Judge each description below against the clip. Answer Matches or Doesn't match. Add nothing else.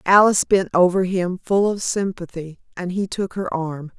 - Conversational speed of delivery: Matches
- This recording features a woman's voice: Matches